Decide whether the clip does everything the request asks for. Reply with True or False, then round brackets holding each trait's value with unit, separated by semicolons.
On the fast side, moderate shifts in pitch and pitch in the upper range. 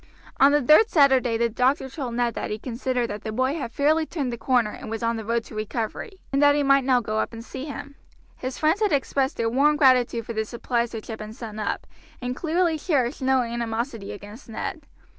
True (230 wpm; 3.7 semitones; 250 Hz)